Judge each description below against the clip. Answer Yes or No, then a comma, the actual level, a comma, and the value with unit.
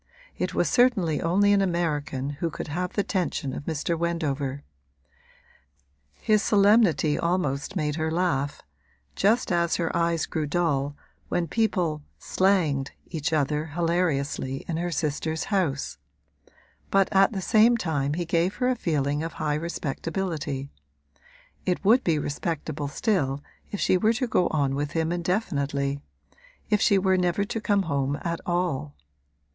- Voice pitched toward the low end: No, medium, 165 Hz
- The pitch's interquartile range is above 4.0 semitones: Yes, average, 4.4 semitones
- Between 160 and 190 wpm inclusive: No, average, 145 wpm